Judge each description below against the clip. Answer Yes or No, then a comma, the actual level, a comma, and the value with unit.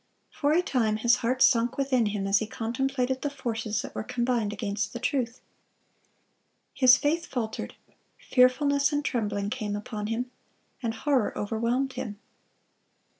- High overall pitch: Yes, high, 240 Hz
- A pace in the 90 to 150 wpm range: Yes, average, 145 wpm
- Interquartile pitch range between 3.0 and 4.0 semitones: Yes, average, 3.4 semitones